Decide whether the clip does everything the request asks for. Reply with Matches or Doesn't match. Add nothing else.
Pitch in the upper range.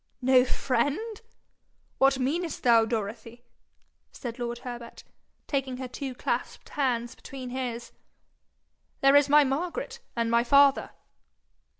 Matches